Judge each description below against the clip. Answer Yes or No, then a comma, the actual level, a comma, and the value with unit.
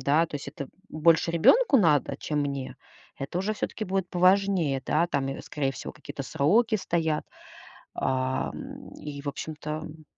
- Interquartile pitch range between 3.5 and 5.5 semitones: Yes, average, 4.1 semitones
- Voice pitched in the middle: Yes, medium, 155 Hz